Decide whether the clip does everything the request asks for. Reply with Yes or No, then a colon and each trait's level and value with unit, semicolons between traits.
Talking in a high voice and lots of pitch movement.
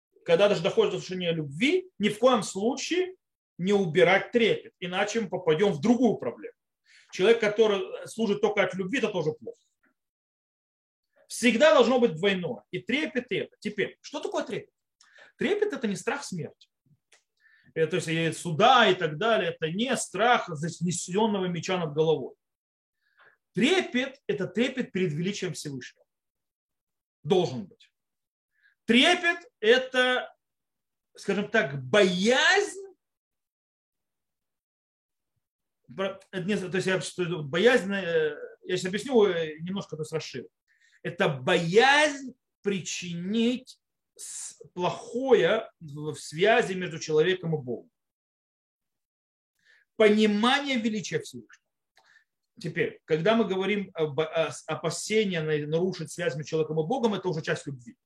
Yes: high, 200 Hz; wide, 6.8 semitones